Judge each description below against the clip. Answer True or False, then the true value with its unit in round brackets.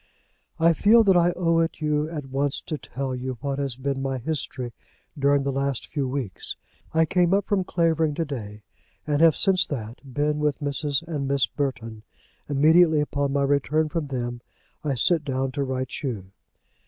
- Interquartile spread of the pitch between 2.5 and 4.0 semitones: True (3.2 semitones)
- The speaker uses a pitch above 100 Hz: True (140 Hz)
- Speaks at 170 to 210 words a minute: True (180 wpm)